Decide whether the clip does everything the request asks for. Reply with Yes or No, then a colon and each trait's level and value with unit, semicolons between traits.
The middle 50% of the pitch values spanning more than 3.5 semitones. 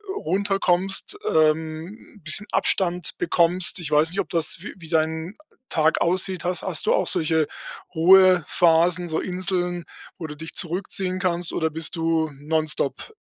No: narrow, 2.4 semitones